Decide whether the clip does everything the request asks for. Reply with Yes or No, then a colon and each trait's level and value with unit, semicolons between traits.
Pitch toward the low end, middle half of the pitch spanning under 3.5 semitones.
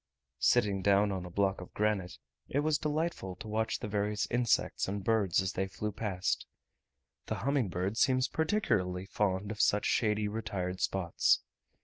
Yes: low, 105 Hz; average, 3.0 semitones